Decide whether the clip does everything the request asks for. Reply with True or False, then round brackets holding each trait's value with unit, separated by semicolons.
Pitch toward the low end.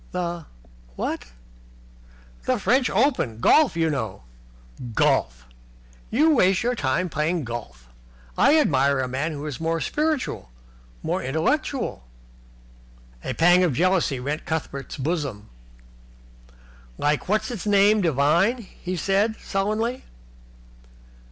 False (170 Hz)